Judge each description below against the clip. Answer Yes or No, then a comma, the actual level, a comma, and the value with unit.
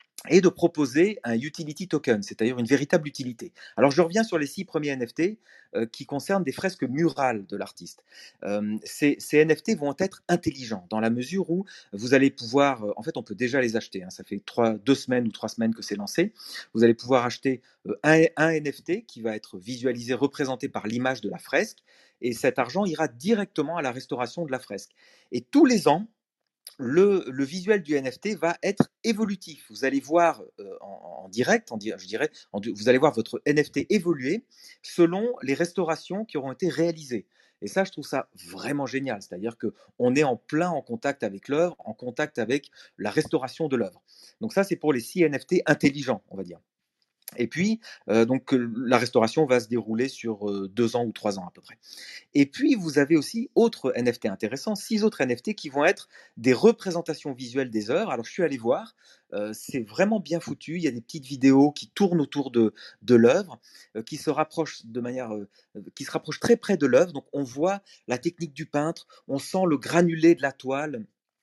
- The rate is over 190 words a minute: Yes, average, 205 wpm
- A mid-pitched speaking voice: Yes, medium, 145 Hz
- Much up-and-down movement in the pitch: Yes, wide, 5.8 semitones